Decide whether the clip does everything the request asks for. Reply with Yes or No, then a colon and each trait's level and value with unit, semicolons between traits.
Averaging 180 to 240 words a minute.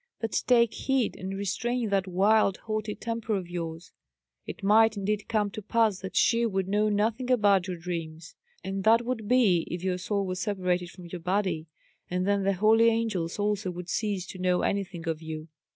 Yes: average, 190 wpm